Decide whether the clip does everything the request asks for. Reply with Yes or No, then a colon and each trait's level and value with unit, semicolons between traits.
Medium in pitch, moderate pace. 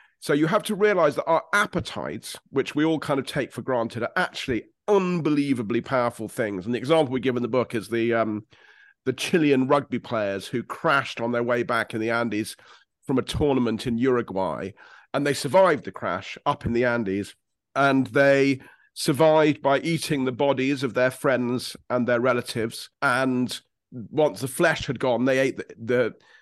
No: low, 130 Hz; average, 185 wpm